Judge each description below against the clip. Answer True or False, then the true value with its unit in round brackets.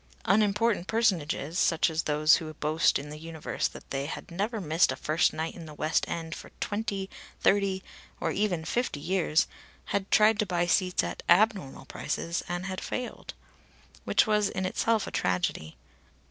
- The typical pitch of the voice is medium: True (175 Hz)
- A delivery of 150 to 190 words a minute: True (170 wpm)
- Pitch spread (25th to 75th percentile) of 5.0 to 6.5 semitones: False (4.5 semitones)